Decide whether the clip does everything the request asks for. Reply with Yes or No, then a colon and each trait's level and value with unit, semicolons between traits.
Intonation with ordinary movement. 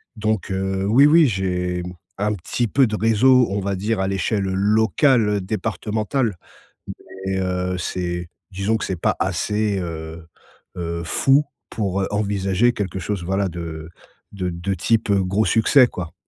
Yes: average, 3.0 semitones